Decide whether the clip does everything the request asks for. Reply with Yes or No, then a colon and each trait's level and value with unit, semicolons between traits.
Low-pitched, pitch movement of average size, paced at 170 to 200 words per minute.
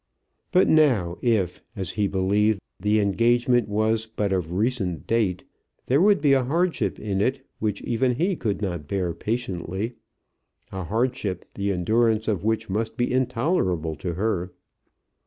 No: low, 110 Hz; average, 4.4 semitones; average, 150 wpm